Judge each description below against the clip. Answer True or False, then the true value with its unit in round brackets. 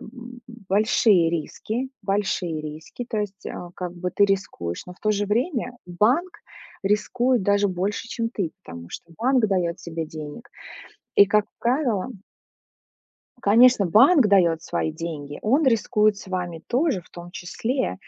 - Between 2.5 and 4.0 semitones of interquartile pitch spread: False (5.3 semitones)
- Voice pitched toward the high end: True (200 Hz)